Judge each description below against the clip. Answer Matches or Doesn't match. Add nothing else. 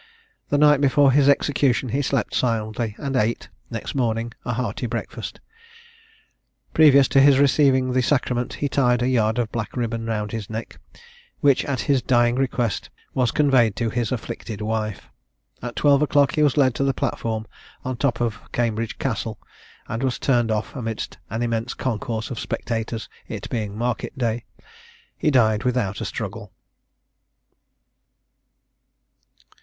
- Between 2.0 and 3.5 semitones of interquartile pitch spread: Matches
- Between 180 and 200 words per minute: Doesn't match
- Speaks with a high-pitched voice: Doesn't match